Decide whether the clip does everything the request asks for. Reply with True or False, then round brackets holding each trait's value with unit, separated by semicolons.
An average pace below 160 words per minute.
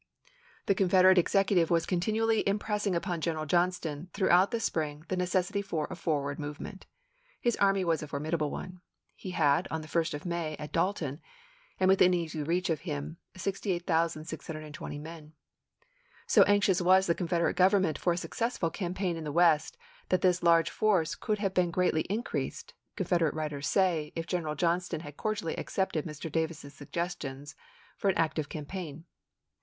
False (165 wpm)